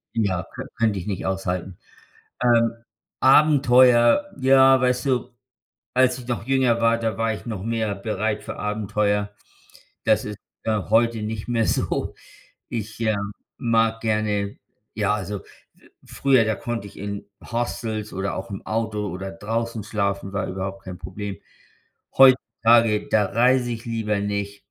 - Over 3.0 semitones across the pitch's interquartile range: No, narrow, 2.6 semitones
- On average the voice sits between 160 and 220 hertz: No, low, 110 Hz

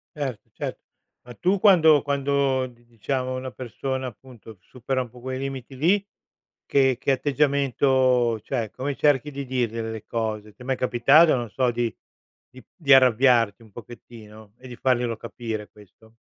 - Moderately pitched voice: No, low, 130 Hz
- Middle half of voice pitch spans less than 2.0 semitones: No, average, 2.8 semitones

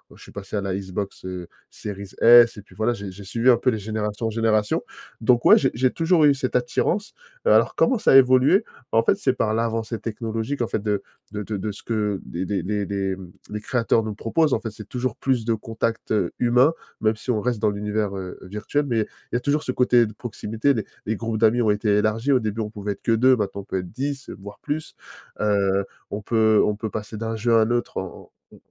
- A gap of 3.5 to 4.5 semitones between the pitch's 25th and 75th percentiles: No, average, 2.8 semitones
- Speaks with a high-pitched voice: No, low, 110 Hz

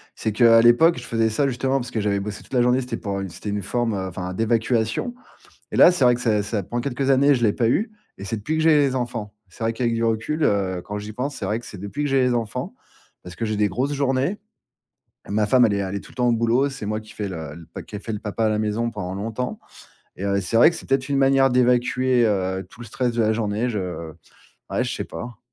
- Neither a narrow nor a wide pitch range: Yes, average, 3.6 semitones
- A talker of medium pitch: No, low, 115 Hz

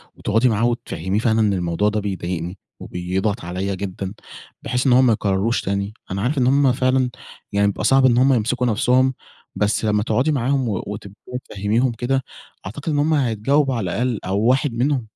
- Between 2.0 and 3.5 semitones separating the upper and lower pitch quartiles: No, average, 4.2 semitones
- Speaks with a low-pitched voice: Yes, low, 115 Hz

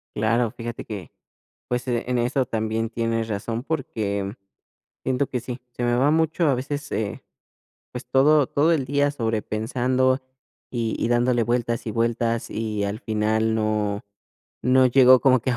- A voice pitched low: Yes, low, 120 Hz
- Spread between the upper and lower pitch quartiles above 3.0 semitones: No, average, 2.7 semitones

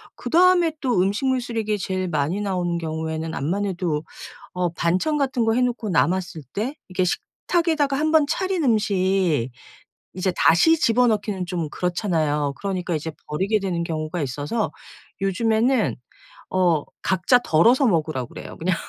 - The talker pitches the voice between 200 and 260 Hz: No, high, 190 Hz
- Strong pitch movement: Yes, wide, 6.1 semitones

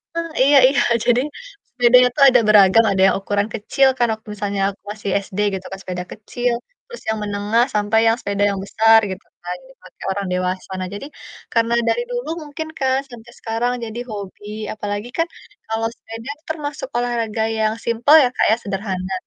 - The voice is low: No, high, 225 Hz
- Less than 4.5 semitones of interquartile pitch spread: Yes, average, 3.2 semitones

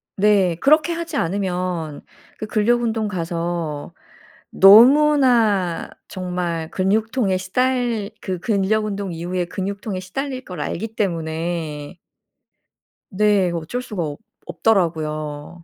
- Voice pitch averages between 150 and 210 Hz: Yes, high, 190 Hz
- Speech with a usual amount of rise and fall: Yes, average, 4.3 semitones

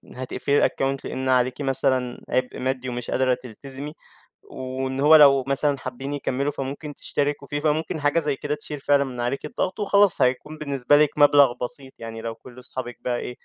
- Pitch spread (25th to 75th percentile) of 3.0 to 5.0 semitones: No, narrow, 2.4 semitones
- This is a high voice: No, low, 135 Hz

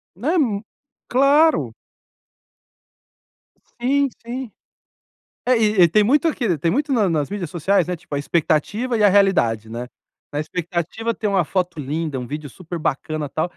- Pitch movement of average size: No, wide, 7.0 semitones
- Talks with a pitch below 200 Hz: Yes, medium, 185 Hz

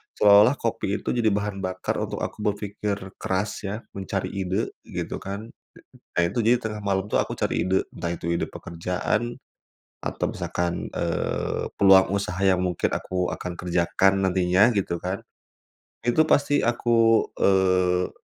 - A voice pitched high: No, very low, 95 Hz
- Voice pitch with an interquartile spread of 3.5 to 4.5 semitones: No, narrow, 2.6 semitones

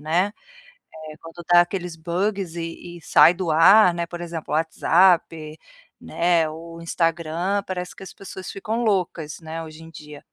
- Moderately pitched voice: Yes, medium, 170 Hz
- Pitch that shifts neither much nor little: No, narrow, 2.0 semitones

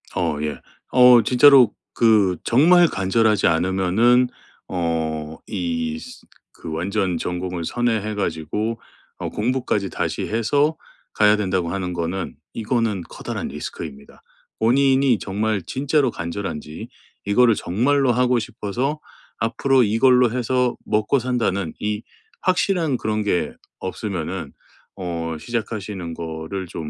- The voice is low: Yes, low, 105 Hz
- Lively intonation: Yes, wide, 5.7 semitones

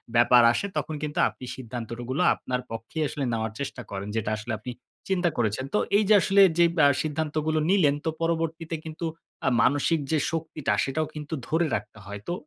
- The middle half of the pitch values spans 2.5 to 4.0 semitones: No, average, 5.0 semitones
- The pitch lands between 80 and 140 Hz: No, medium, 150 Hz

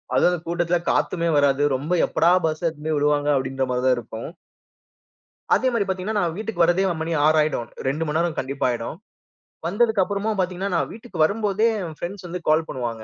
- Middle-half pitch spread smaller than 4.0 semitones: No, average, 4.7 semitones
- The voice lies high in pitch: No, medium, 170 Hz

